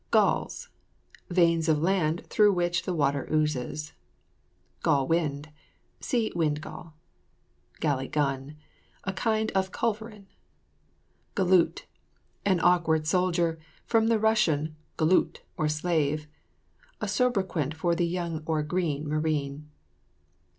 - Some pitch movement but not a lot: Yes, average, 3.5 semitones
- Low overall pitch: No, medium, 165 Hz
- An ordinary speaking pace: No, slow, 110 wpm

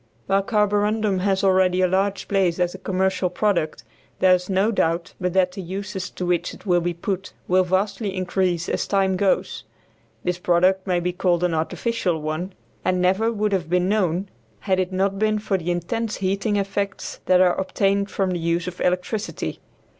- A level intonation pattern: Yes, narrow, 1.8 semitones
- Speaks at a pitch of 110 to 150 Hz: No, medium, 185 Hz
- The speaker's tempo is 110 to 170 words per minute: No, average, 190 wpm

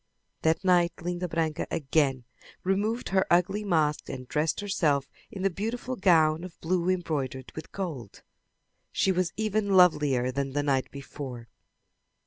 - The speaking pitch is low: No, medium, 165 Hz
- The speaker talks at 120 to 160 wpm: Yes, average, 140 wpm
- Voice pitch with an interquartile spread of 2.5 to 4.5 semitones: No, average, 4.9 semitones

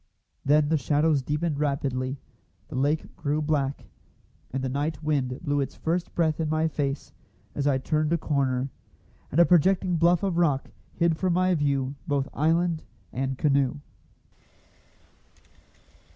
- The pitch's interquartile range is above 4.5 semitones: No, average, 2.9 semitones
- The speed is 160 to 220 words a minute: No, average, 145 wpm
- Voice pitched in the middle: Yes, medium, 150 Hz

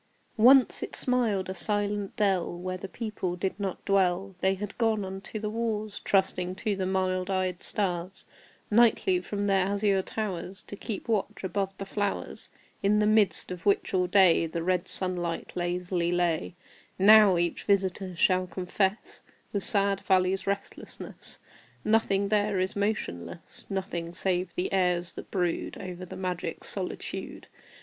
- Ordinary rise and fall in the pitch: No, narrow, 2.0 semitones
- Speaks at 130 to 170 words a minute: Yes, average, 155 wpm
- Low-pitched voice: No, high, 190 Hz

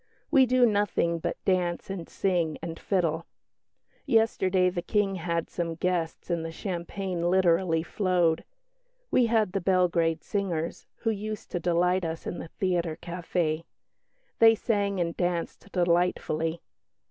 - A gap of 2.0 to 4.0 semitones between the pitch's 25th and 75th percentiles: Yes, average, 2.7 semitones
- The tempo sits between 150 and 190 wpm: No, slow, 135 wpm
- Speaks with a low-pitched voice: No, medium, 180 Hz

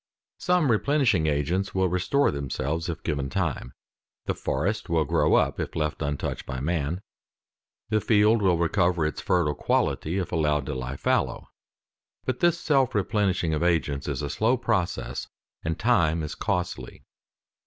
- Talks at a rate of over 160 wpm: No, average, 155 wpm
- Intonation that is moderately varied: No, wide, 5.9 semitones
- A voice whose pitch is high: No, very low, 85 Hz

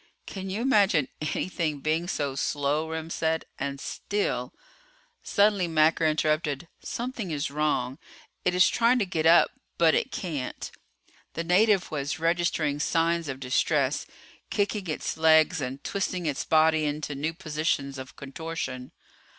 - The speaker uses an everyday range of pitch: Yes, average, 3.5 semitones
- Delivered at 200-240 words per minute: No, average, 140 wpm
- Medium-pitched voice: Yes, medium, 160 Hz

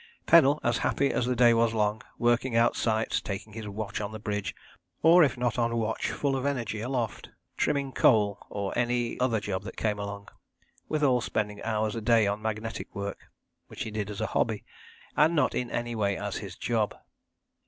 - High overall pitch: No, low, 115 Hz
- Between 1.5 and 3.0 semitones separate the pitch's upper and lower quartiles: Yes, average, 2.7 semitones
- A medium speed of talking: Yes, average, 195 wpm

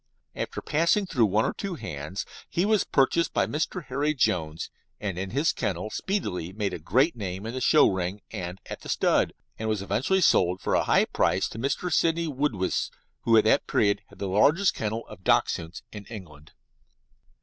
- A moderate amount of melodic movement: No, wide, 8.0 semitones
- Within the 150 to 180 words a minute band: No, average, 190 wpm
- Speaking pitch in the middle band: No, low, 110 Hz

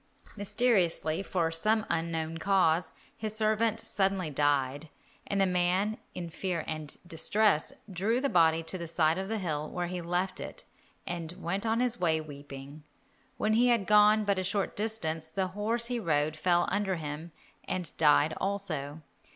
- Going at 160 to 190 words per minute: Yes, average, 165 wpm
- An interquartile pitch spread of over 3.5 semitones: Yes, average, 4.5 semitones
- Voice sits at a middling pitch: Yes, medium, 180 Hz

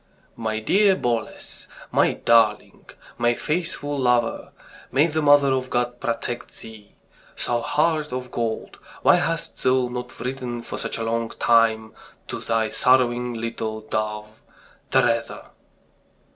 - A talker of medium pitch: No, low, 120 Hz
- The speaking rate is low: Yes, slow, 130 wpm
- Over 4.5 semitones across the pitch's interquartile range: No, narrow, 2.5 semitones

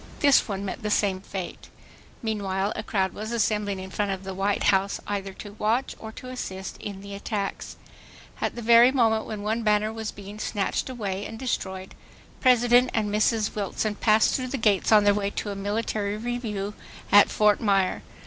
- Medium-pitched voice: No, high, 210 Hz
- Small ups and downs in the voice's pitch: Yes, narrow, 2.0 semitones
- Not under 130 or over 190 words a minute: Yes, average, 185 wpm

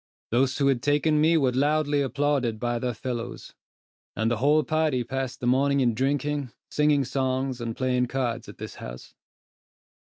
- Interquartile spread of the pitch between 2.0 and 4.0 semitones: Yes, average, 3.0 semitones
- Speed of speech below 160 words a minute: No, average, 165 wpm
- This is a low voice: Yes, low, 130 Hz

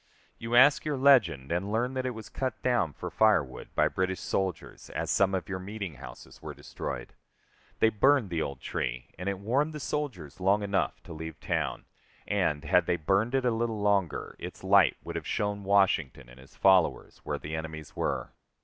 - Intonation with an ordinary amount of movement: No, wide, 6.2 semitones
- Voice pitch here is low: Yes, low, 100 Hz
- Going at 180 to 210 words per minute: Yes, average, 195 wpm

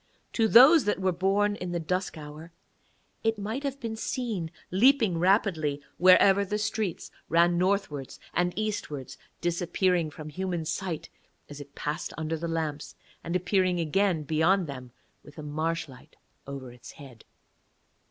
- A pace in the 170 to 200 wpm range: No, average, 150 wpm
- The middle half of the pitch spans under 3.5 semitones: No, average, 4.5 semitones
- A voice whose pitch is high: No, medium, 175 Hz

